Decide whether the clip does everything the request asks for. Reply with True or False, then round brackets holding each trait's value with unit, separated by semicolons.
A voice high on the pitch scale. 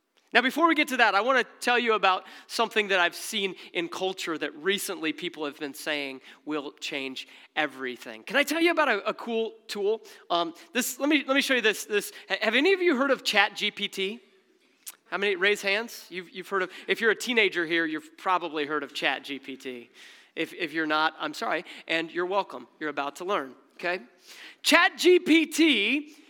True (195 Hz)